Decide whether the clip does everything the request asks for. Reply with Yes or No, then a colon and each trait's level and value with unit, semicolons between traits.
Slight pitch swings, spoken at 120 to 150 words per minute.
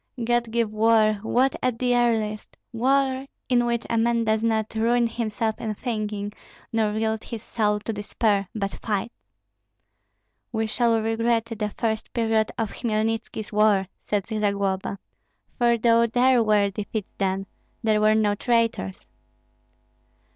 Yes: narrow, 1.7 semitones; average, 140 wpm